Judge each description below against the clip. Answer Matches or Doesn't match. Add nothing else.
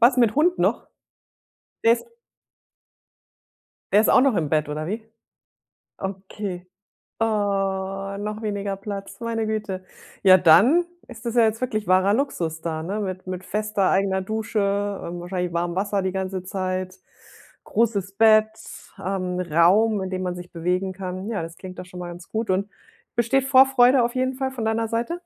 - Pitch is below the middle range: Doesn't match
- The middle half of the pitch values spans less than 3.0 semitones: Doesn't match